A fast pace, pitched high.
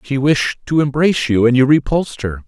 No: fast, 220 wpm; low, 135 Hz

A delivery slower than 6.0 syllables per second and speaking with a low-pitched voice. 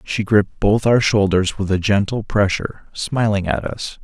Yes: 4.7 syllables/s; low, 100 Hz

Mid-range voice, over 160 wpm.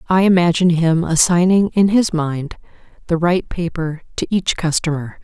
No: medium, 170 Hz; average, 150 wpm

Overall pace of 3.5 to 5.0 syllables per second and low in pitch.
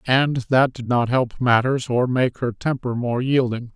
Yes: 4.1 syllables/s; low, 125 Hz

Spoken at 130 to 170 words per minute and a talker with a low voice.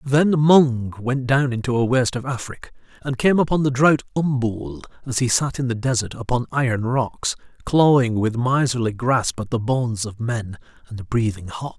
No: average, 185 wpm; low, 125 Hz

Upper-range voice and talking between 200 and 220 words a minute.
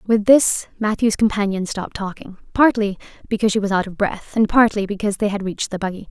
Yes: high, 205 Hz; fast, 205 wpm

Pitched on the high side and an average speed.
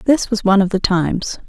No: high, 200 Hz; fast, 245 wpm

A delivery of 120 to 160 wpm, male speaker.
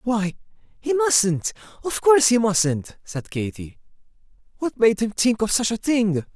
Yes: average, 150 wpm; male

